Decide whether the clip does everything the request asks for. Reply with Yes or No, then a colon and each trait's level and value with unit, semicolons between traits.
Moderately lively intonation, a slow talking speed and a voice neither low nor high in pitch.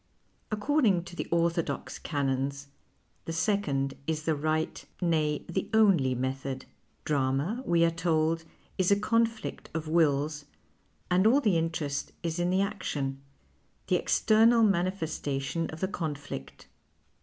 Yes: average, 4.8 semitones; slow, 130 wpm; medium, 165 Hz